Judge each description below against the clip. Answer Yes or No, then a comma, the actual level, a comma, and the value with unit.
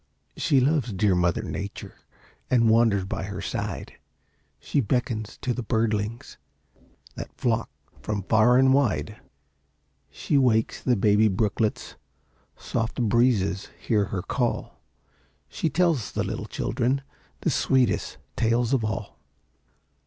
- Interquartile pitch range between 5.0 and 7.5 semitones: No, average, 3.3 semitones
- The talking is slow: Yes, slow, 125 wpm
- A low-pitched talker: Yes, low, 115 Hz